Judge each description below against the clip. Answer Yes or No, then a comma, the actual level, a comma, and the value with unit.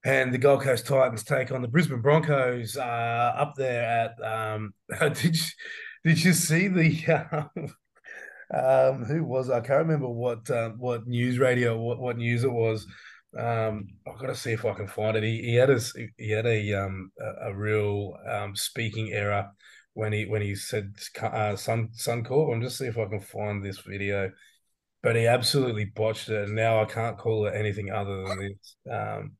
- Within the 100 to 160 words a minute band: No, average, 195 wpm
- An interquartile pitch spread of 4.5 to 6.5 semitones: No, average, 3.7 semitones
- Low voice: Yes, low, 115 Hz